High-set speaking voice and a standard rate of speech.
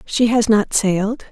Yes: high, 215 Hz; average, 185 wpm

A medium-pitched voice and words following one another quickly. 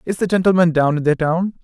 Yes: medium, 170 Hz; fast, 255 wpm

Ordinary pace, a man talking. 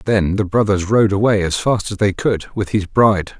No: fast, 230 wpm; male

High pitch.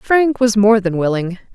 Yes: high, 215 Hz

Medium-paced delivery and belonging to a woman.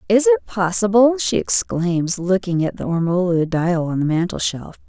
Yes: average, 160 wpm; female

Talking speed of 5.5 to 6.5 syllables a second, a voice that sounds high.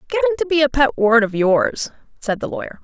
Yes: 5.6 syllables/s; high, 245 Hz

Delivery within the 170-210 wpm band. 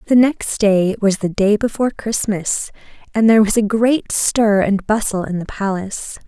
Yes: average, 180 wpm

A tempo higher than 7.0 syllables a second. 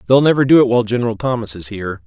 Yes: 8.1 syllables/s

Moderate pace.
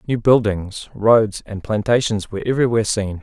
Yes: average, 150 wpm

